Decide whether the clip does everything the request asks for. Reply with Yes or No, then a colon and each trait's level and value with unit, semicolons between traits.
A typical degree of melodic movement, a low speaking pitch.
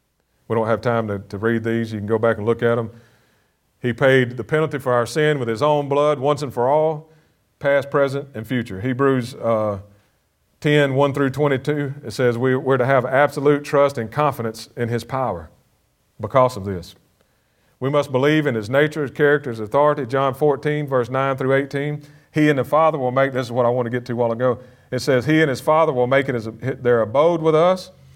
Yes: average, 3.8 semitones; low, 130 Hz